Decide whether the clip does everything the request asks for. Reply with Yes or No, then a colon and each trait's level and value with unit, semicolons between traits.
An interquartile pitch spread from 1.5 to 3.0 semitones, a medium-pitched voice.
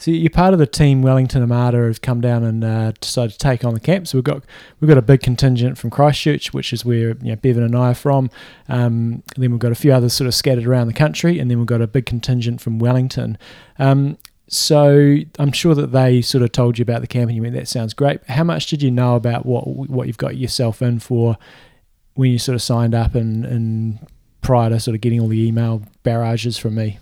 No: narrow, 2.6 semitones; low, 125 Hz